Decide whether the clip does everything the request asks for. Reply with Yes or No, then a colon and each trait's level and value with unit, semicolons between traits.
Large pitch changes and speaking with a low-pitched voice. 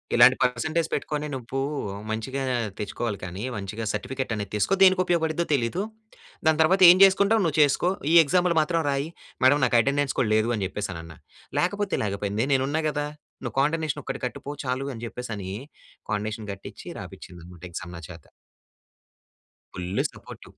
Yes: wide, 7.1 semitones; low, 130 Hz